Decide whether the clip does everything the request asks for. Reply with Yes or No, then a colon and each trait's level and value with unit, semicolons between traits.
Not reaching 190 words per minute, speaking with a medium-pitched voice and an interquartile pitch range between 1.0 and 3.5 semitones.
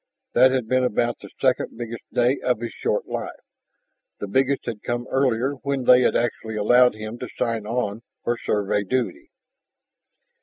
No: average, 165 wpm; low, 120 Hz; narrow, 2.5 semitones